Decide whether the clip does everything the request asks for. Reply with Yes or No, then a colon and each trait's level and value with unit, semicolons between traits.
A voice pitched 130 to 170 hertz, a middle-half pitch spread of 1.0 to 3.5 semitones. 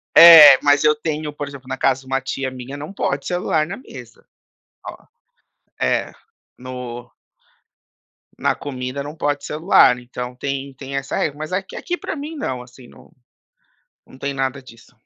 Yes: medium, 140 Hz; average, 2.8 semitones